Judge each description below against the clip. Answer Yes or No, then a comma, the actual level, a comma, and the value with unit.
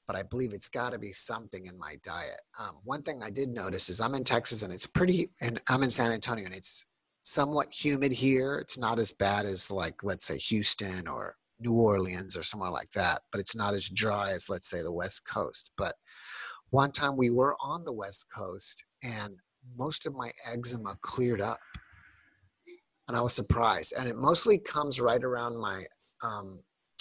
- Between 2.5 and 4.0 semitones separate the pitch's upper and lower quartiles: No, average, 4.6 semitones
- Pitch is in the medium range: No, low, 115 Hz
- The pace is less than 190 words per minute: No, average, 200 wpm